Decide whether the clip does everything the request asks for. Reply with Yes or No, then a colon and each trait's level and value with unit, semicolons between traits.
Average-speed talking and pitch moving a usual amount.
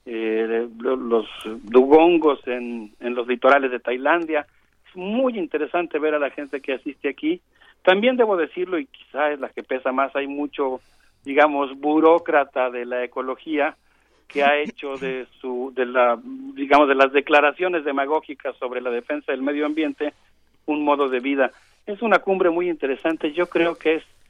Yes: average, 165 wpm; average, 3.5 semitones